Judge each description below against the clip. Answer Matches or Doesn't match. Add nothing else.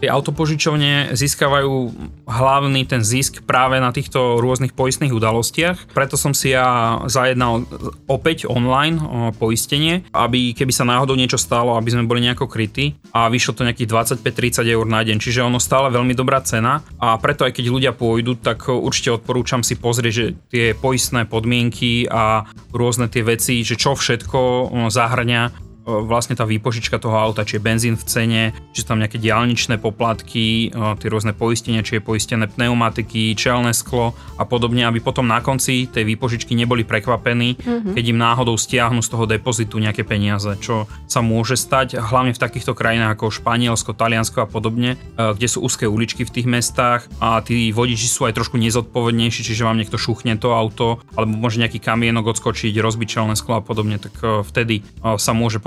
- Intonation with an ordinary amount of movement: Doesn't match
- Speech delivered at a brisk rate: Matches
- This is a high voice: Doesn't match